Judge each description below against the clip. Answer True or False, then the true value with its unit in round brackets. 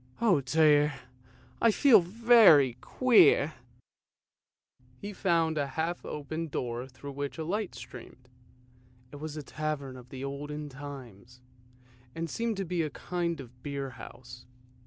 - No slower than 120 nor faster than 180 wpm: True (140 wpm)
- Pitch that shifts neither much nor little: True (4.3 semitones)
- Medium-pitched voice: True (150 Hz)